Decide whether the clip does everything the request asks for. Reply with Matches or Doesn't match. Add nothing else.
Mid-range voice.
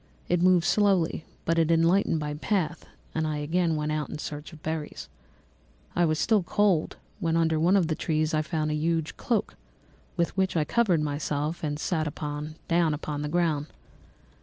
Matches